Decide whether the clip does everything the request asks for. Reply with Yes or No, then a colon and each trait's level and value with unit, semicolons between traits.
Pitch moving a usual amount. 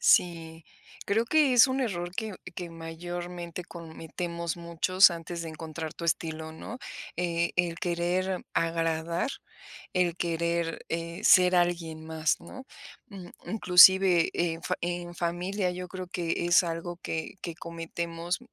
No: narrow, 1.4 semitones